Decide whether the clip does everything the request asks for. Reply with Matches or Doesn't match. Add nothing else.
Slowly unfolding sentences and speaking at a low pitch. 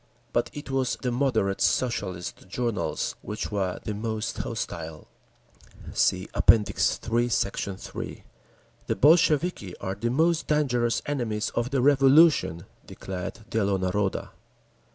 Matches